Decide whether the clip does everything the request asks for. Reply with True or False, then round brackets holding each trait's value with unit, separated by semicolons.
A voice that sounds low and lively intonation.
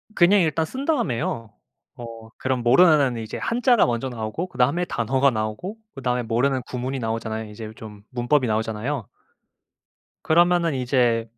True (125 Hz; 5.7 semitones)